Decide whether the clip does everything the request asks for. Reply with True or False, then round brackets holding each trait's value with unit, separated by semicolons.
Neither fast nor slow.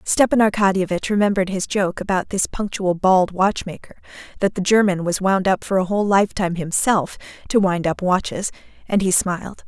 True (175 wpm)